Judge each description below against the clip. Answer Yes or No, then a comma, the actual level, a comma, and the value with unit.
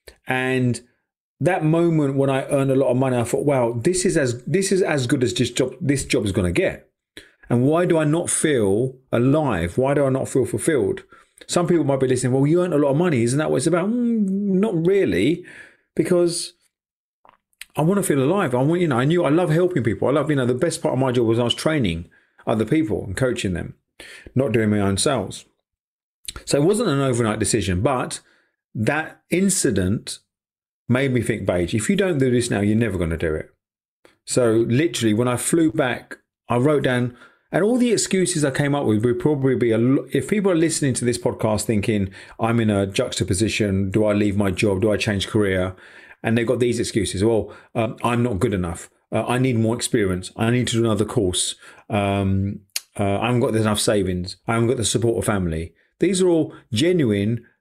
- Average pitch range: No, wide, 6.0 semitones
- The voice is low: Yes, low, 125 Hz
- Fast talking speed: Yes, fast, 220 wpm